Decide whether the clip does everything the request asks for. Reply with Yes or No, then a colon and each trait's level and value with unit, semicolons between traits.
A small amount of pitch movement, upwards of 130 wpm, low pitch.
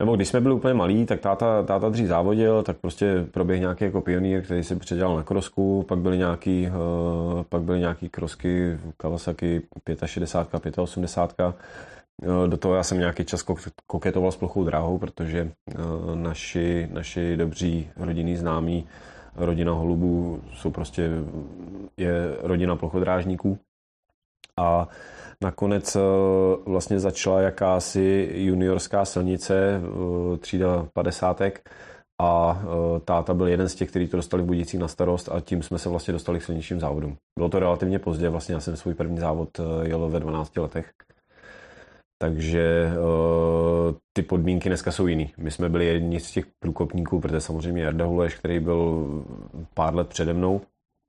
Yes: narrow, 1.7 semitones; average, 140 wpm; very low, 85 Hz